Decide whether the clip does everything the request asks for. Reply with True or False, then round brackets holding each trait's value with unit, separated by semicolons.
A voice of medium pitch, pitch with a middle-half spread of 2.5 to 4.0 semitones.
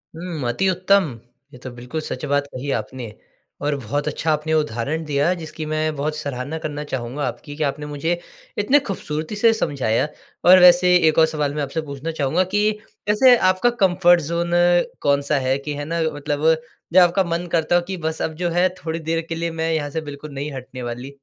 True (155 Hz; 3.2 semitones)